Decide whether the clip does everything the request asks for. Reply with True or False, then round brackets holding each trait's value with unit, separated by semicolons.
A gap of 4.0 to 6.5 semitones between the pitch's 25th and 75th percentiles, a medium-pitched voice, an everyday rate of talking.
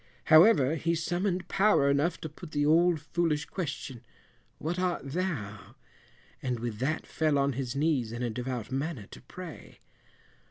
True (4.7 semitones; 150 Hz; 155 wpm)